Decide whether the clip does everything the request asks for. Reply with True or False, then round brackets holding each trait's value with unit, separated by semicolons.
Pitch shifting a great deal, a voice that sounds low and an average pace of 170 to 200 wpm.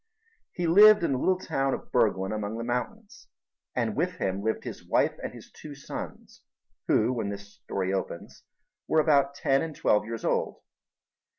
True (6.8 semitones; 125 Hz; 175 wpm)